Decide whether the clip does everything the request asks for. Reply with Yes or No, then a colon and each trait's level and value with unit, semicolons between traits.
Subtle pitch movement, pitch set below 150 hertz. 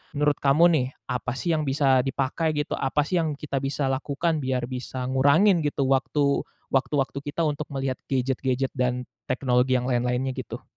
Yes: narrow, 2.3 semitones; low, 135 Hz